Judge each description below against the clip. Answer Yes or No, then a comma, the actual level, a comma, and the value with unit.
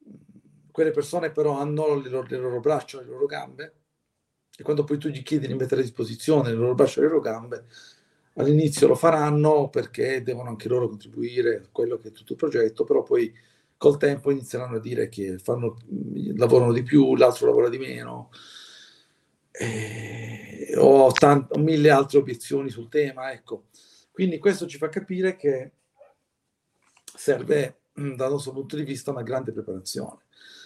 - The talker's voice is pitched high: No, medium, 140 Hz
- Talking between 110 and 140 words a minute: No, average, 160 wpm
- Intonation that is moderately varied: Yes, average, 4.1 semitones